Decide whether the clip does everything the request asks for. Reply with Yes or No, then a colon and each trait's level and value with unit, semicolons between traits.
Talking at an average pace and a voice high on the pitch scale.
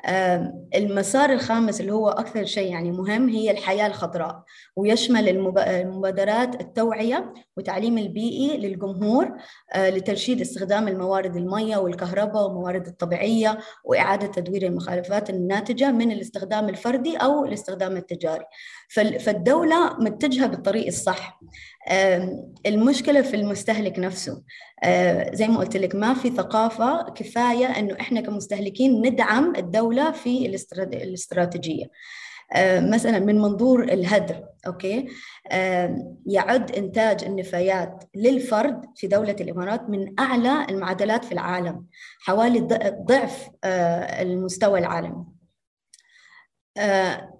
No: slow, 100 wpm; high, 205 Hz